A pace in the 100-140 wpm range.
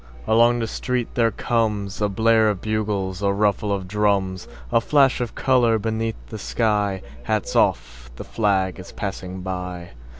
Yes: slow, 135 wpm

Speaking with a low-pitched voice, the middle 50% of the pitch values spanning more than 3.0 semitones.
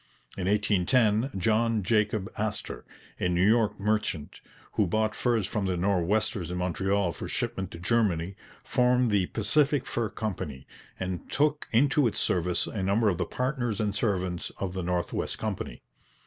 Yes: low, 105 Hz; average, 3.8 semitones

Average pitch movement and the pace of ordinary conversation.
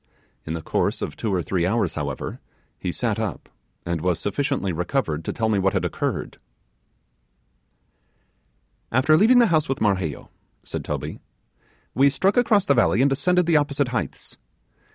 No: wide, 8.8 semitones; average, 160 wpm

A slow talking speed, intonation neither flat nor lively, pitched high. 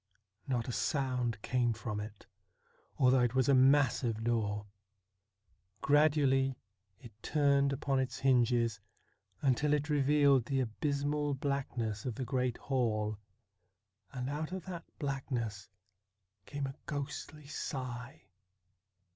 No: slow, 115 wpm; average, 3.1 semitones; low, 130 Hz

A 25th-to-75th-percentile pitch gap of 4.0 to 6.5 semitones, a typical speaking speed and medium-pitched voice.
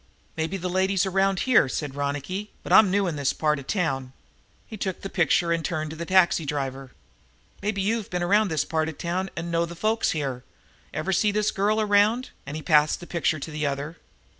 No: average, 4.5 semitones; fast, 215 wpm; medium, 170 Hz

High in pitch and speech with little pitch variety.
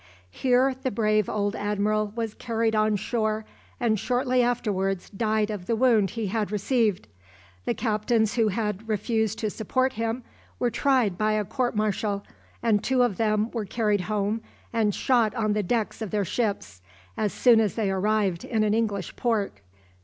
Yes: high, 215 Hz; narrow, 2.0 semitones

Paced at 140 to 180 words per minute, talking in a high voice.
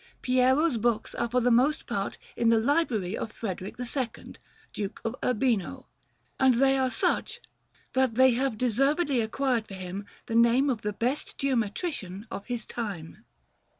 Yes: average, 155 wpm; high, 240 Hz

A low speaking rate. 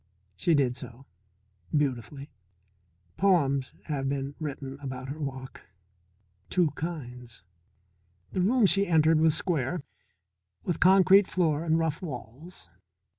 Yes: slow, 115 wpm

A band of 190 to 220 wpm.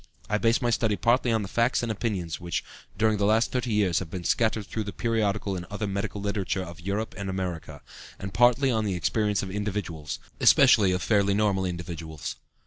Yes: average, 200 wpm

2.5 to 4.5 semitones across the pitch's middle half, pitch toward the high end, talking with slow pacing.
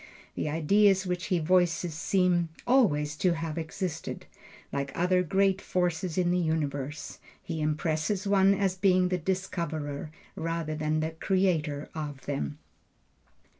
No: average, 3.2 semitones; medium, 170 Hz; slow, 130 wpm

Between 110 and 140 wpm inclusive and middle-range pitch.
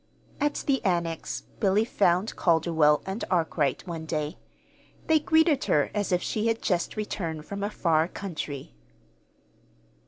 Yes: slow, 135 wpm; medium, 180 Hz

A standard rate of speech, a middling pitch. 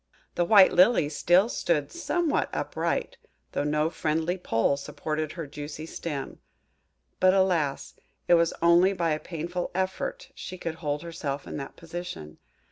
Yes: average, 145 wpm; medium, 165 Hz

